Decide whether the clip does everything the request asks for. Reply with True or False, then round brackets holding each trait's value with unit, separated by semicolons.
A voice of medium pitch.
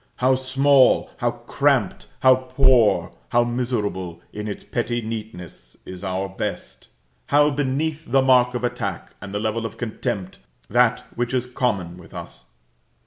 False (120 Hz)